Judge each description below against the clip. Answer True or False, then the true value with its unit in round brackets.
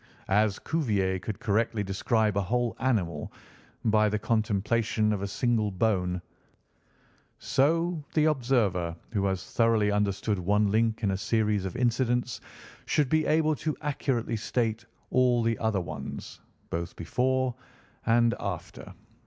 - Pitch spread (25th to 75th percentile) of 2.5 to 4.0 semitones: True (3.4 semitones)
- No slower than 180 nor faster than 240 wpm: False (135 wpm)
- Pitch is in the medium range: False (110 Hz)